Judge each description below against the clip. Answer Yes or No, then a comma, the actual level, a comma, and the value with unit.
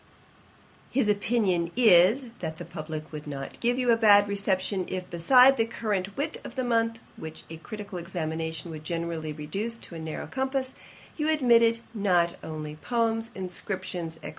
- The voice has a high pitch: Yes, high, 195 Hz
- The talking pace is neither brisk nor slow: Yes, average, 165 wpm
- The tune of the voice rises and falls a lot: Yes, wide, 5.9 semitones